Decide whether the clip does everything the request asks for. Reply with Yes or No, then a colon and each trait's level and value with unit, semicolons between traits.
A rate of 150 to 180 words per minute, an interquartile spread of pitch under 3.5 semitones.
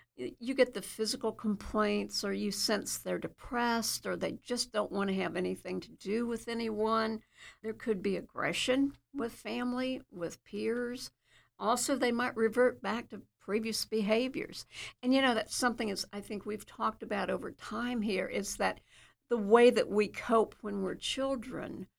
Yes: average, 170 wpm; average, 2.8 semitones